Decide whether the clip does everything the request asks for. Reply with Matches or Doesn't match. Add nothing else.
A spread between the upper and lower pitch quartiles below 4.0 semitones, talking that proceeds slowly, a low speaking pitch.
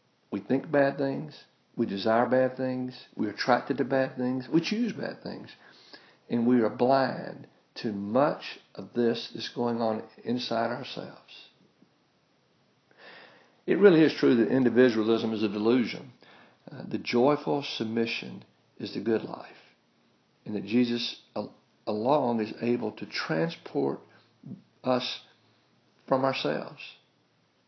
Matches